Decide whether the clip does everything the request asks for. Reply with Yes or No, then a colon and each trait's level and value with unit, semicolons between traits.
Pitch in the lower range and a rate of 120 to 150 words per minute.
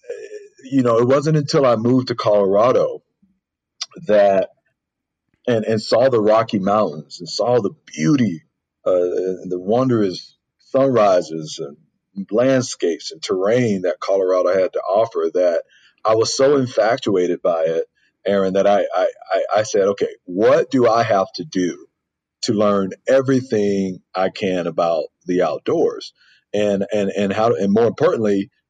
Yes: low, 120 Hz; average, 145 wpm